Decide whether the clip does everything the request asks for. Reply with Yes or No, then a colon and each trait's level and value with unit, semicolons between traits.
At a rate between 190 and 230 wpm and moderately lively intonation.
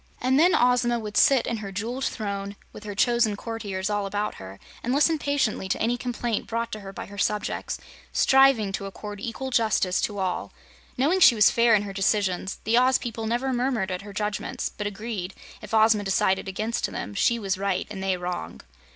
Yes: average, 200 wpm; average, 3.4 semitones